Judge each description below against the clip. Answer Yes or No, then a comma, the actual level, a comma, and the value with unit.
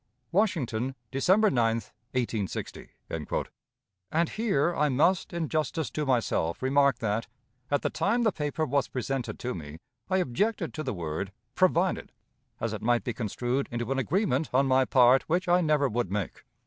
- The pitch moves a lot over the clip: Yes, wide, 5.9 semitones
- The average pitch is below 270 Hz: Yes, low, 135 Hz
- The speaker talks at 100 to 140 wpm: No, average, 160 wpm